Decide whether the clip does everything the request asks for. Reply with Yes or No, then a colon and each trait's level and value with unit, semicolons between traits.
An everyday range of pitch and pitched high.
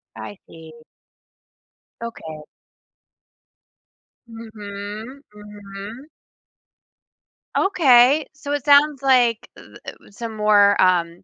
Yes: average, 4.6 semitones; high, 220 Hz